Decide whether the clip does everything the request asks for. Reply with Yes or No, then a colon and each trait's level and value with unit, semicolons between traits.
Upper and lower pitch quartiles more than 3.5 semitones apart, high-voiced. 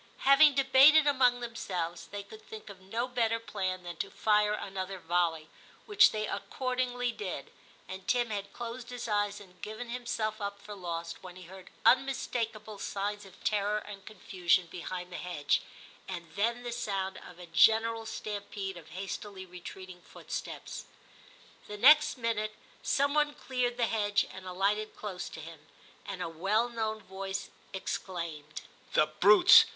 Yes: average, 4.1 semitones; high, 205 Hz